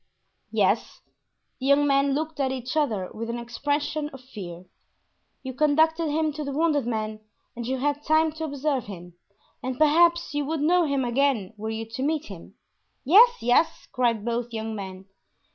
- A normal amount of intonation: Yes, average, 4.9 semitones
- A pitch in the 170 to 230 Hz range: No, very high, 275 Hz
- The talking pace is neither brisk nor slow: Yes, average, 175 wpm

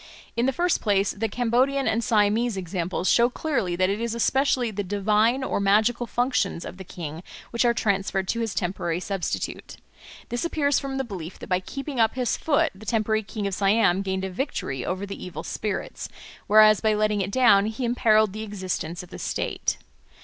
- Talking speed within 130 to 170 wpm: No, average, 195 wpm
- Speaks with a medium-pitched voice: No, high, 215 Hz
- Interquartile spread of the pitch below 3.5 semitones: No, average, 3.9 semitones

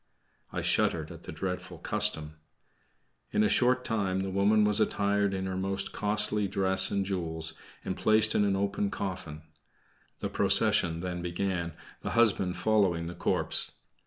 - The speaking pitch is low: Yes, very low, 95 Hz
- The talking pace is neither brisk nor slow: Yes, average, 155 wpm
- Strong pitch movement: No, narrow, 2.5 semitones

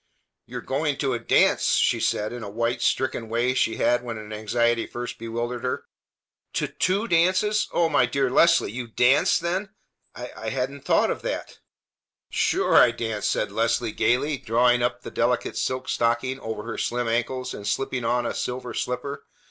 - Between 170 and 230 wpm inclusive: Yes, average, 180 wpm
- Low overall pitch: Yes, low, 120 Hz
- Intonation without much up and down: Yes, narrow, 2.2 semitones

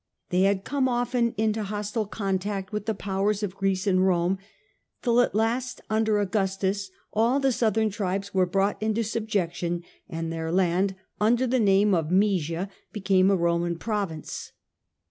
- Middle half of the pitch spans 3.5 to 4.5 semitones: No, average, 2.7 semitones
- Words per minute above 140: Yes, average, 155 wpm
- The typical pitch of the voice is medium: No, high, 200 Hz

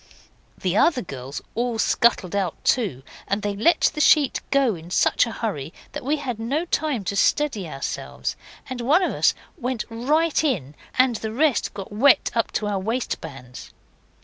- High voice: Yes, high, 230 Hz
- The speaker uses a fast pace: No, average, 175 wpm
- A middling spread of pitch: No, wide, 5.9 semitones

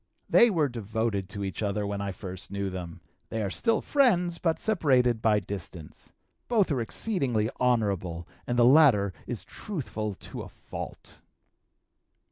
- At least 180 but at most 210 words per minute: No, average, 150 wpm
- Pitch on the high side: No, low, 110 Hz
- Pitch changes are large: Yes, wide, 6.8 semitones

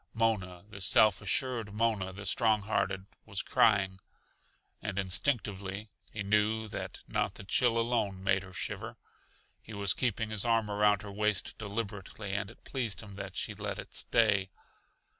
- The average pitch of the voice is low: Yes, low, 105 Hz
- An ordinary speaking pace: Yes, average, 160 wpm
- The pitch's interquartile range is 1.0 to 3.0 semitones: Yes, narrow, 2.4 semitones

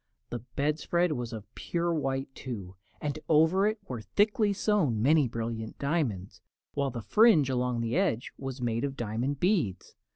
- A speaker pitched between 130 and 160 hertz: Yes, low, 135 Hz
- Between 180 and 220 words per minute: No, average, 160 wpm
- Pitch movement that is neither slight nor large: No, wide, 5.7 semitones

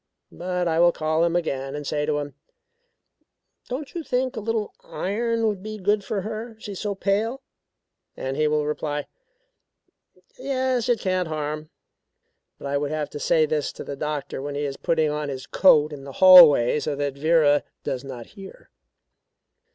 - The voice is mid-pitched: Yes, medium, 160 Hz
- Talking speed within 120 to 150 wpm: No, average, 180 wpm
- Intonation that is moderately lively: No, wide, 6.0 semitones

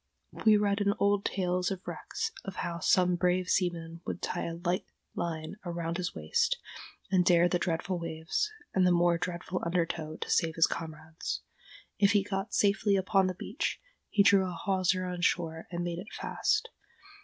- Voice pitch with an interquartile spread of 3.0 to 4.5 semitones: No, narrow, 2.4 semitones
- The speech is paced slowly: No, average, 180 wpm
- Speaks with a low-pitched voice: No, medium, 180 Hz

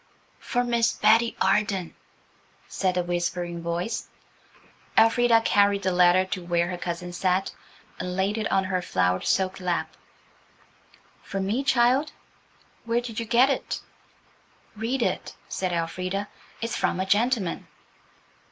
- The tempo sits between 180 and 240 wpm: No, slow, 135 wpm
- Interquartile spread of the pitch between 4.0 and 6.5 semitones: Yes, average, 4.3 semitones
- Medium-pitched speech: No, high, 195 Hz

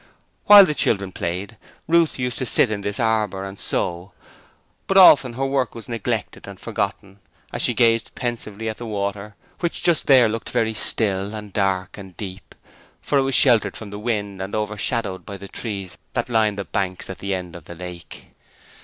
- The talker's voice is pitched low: Yes, low, 105 Hz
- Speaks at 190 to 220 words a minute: Yes, average, 195 wpm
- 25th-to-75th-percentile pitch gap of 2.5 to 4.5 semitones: Yes, average, 3.3 semitones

